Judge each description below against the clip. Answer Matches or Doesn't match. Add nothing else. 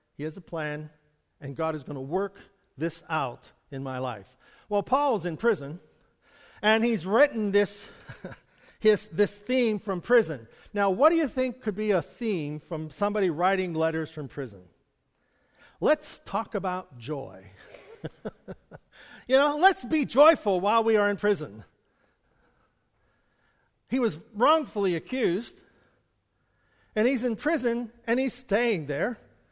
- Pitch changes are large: Matches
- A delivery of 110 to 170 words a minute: Matches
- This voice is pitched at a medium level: Doesn't match